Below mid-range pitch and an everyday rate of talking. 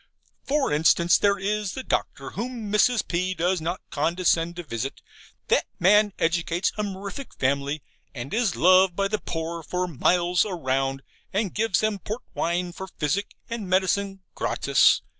No: medium, 180 Hz; average, 155 wpm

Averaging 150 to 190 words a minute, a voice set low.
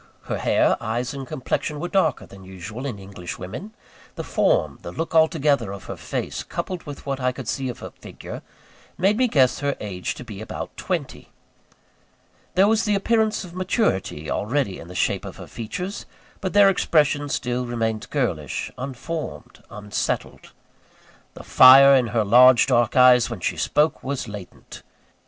Yes: average, 170 wpm; low, 130 Hz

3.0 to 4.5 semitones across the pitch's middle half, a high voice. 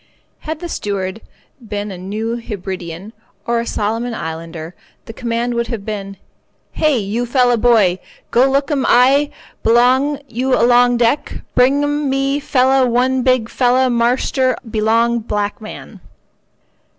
Yes: average, 3.4 semitones; high, 235 Hz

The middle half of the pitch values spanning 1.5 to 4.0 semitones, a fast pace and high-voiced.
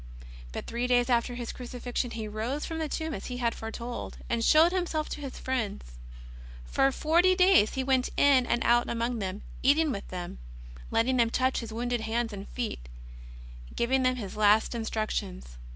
No: average, 3.0 semitones; average, 185 wpm; high, 240 Hz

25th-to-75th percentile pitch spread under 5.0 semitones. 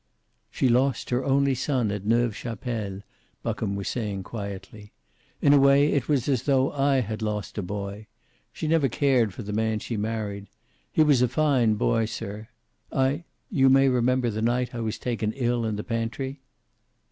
Yes: average, 3.9 semitones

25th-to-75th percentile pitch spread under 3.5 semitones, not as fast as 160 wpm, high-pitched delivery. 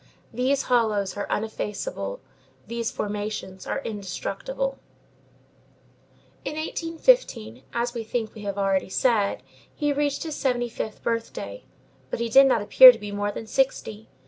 No: average, 5.0 semitones; average, 140 wpm; high, 230 Hz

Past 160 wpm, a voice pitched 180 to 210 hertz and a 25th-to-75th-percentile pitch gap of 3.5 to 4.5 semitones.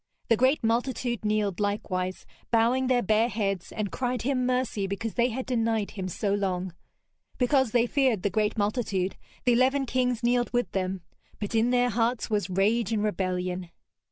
No: average, 170 wpm; high, 225 Hz; average, 3.8 semitones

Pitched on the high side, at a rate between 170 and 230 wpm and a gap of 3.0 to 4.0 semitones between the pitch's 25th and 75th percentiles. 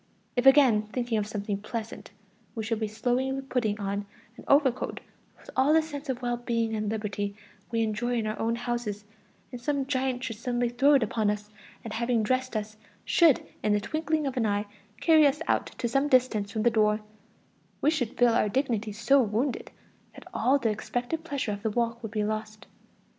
Yes: high, 235 Hz; average, 195 wpm; average, 3.5 semitones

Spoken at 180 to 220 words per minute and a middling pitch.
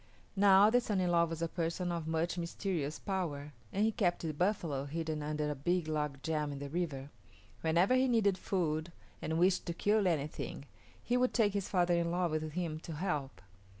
Yes: average, 200 wpm; medium, 170 Hz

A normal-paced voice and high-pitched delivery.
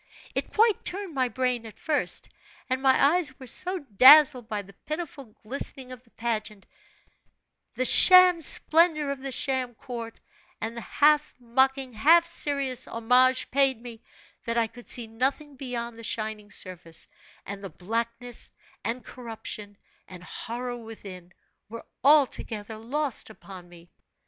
Yes: average, 145 wpm; high, 245 Hz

